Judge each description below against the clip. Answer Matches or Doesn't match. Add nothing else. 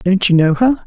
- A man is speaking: Matches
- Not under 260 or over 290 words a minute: Matches